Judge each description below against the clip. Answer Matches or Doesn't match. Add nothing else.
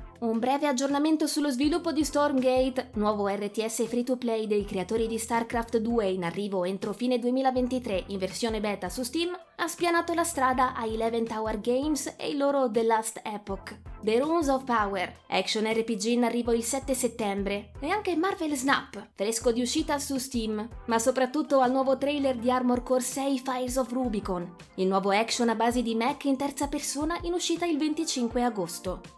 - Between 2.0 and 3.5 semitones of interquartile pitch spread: Doesn't match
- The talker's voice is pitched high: Matches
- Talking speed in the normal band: Doesn't match